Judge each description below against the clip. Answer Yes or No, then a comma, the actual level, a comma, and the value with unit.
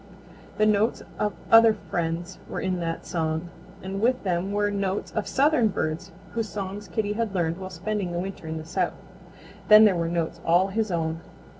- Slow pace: No, average, 185 wpm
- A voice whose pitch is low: No, high, 190 Hz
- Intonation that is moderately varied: Yes, average, 3.8 semitones